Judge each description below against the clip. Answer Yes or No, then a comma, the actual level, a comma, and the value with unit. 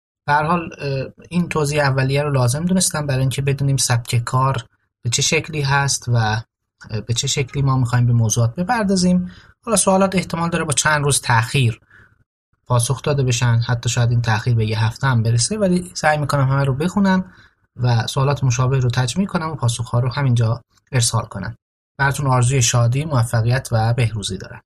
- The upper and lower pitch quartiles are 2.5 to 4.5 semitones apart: Yes, average, 3.8 semitones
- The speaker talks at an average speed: No, fast, 175 wpm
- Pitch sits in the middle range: No, low, 130 Hz